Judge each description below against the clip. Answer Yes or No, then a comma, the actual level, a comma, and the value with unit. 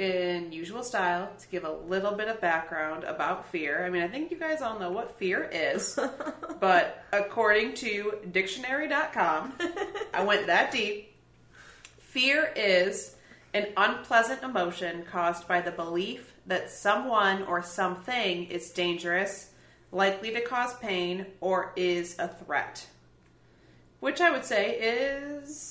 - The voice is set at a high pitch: Yes, high, 195 Hz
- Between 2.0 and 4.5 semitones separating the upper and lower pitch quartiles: No, wide, 5.6 semitones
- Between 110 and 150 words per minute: Yes, average, 140 wpm